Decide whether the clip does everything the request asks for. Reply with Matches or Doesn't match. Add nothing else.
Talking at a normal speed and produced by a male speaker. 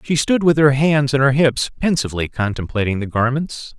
Matches